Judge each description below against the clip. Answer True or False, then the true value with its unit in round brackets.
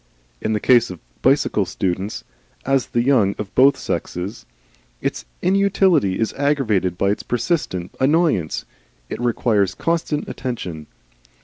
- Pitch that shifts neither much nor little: False (6.6 semitones)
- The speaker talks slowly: True (130 wpm)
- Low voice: True (120 Hz)